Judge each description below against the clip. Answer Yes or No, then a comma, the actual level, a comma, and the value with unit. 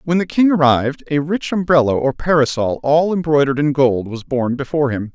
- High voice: No, medium, 145 Hz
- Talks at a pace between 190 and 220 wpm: Yes, average, 200 wpm